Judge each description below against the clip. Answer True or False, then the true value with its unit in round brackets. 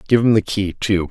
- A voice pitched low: True (105 Hz)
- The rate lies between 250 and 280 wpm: True (270 wpm)